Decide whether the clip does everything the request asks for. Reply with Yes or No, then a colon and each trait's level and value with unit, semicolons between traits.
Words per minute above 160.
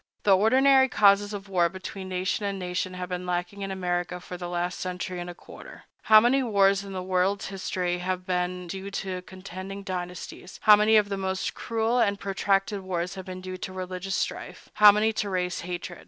Yes: average, 200 wpm